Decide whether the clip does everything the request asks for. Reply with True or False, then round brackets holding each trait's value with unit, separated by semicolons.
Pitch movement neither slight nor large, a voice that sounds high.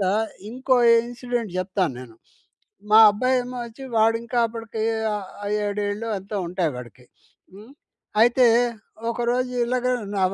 True (3.4 semitones; 225 Hz)